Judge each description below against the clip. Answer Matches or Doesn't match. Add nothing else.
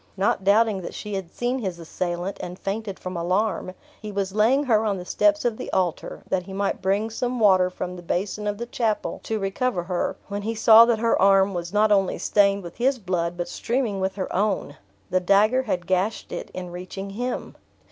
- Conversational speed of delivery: Doesn't match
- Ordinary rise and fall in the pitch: Matches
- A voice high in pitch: Matches